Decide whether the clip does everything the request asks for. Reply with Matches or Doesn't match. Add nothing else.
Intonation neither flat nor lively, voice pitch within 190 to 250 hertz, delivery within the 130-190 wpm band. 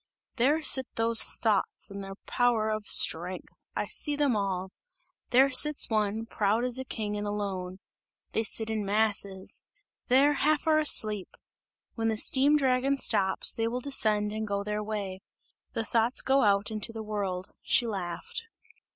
Matches